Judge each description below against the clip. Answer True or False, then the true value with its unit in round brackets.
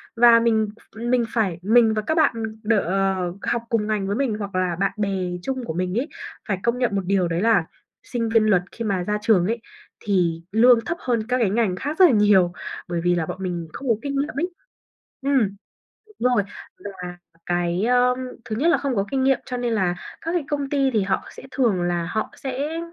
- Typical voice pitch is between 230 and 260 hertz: False (220 Hz)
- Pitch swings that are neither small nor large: True (5.0 semitones)